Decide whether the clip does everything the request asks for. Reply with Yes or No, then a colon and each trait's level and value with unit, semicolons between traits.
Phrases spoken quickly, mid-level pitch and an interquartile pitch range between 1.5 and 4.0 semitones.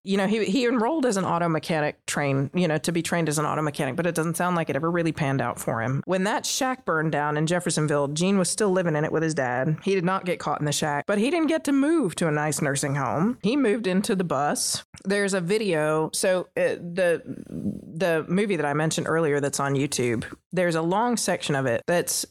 No: fast, 250 wpm; medium, 170 Hz; average, 4.5 semitones